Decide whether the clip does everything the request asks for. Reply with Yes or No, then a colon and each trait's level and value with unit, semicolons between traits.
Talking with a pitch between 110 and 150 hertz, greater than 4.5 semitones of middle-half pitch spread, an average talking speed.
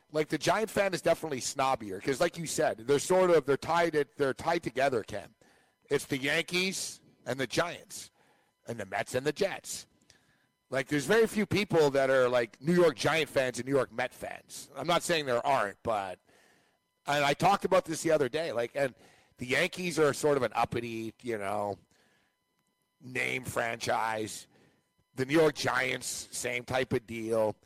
Yes: medium, 140 Hz; average, 5.1 semitones; average, 185 wpm